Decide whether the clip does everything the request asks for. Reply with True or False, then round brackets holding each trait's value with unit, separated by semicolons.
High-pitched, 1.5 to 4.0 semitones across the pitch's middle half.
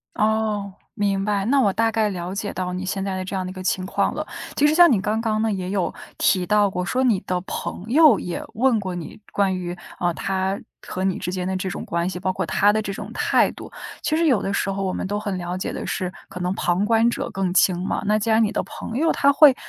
True (195 Hz; 2.9 semitones)